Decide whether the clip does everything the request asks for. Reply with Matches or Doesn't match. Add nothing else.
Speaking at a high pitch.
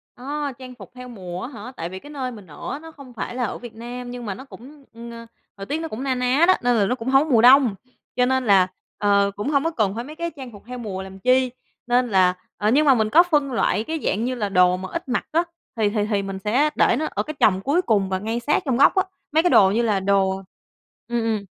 Matches